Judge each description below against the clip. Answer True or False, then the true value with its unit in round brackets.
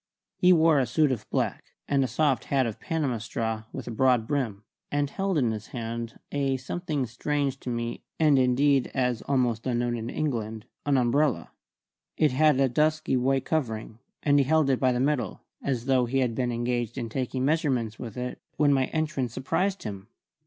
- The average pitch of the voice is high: False (130 Hz)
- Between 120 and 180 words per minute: False (195 wpm)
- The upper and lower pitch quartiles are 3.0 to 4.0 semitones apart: True (3.5 semitones)